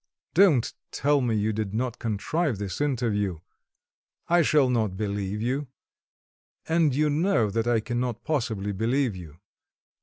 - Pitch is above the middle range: No, low, 120 Hz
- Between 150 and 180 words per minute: No, average, 140 wpm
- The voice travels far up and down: Yes, wide, 5.7 semitones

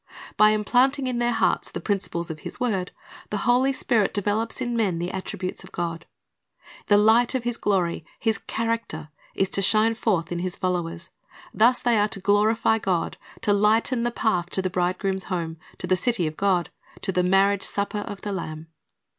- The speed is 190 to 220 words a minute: Yes, average, 195 wpm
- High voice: Yes, high, 205 Hz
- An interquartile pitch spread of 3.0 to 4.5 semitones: Yes, average, 3.9 semitones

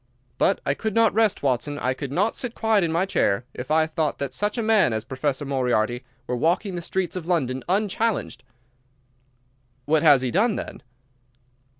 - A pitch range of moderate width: No, wide, 7.5 semitones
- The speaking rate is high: No, average, 185 wpm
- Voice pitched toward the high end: No, medium, 160 Hz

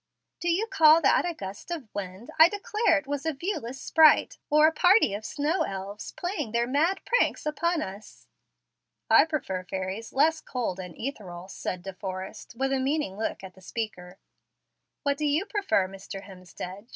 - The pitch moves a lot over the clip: Yes, wide, 8.7 semitones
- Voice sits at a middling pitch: No, very high, 260 Hz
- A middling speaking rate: Yes, average, 175 wpm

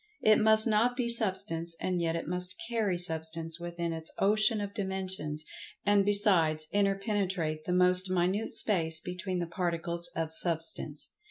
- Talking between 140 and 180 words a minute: Yes, average, 150 wpm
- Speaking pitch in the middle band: Yes, medium, 180 Hz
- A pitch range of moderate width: Yes, average, 3.5 semitones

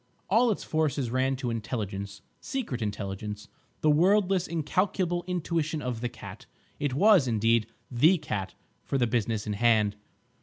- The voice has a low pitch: Yes, low, 130 Hz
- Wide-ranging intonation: Yes, wide, 7.2 semitones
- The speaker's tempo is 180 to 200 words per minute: No, average, 140 wpm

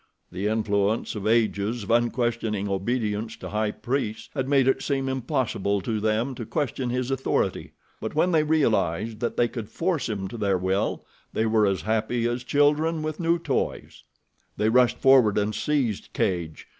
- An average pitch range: Yes, average, 4.1 semitones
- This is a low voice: Yes, low, 115 Hz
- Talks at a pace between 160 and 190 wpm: Yes, average, 170 wpm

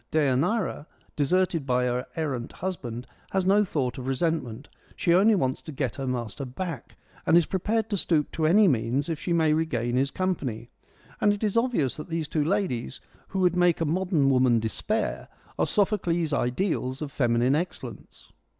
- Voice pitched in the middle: Yes, medium, 155 Hz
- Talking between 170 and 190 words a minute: Yes, average, 175 wpm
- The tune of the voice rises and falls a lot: Yes, wide, 6.2 semitones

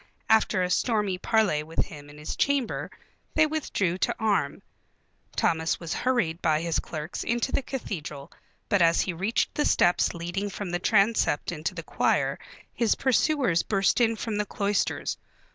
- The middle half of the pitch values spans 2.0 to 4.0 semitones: No, average, 5.2 semitones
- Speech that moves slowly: No, average, 160 wpm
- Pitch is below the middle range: No, high, 195 Hz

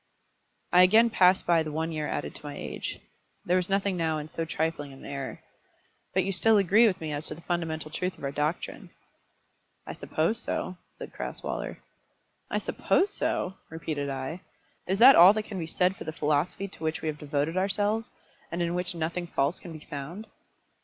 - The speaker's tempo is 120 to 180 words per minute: No, average, 195 wpm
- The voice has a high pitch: No, medium, 170 Hz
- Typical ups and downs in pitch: Yes, average, 3.6 semitones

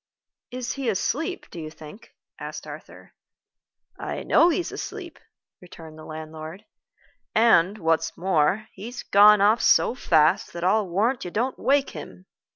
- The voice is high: Yes, high, 195 Hz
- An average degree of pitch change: No, wide, 6.5 semitones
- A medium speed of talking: Yes, average, 145 wpm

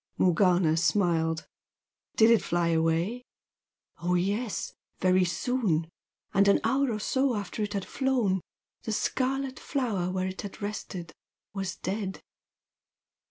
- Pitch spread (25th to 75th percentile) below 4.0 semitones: No, average, 4.4 semitones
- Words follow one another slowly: Yes, slow, 125 wpm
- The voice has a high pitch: Yes, high, 195 Hz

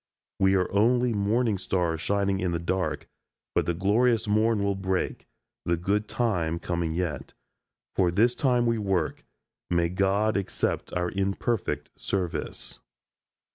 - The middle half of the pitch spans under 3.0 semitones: No, average, 3.4 semitones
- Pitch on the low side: Yes, very low, 95 Hz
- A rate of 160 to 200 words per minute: No, slow, 135 wpm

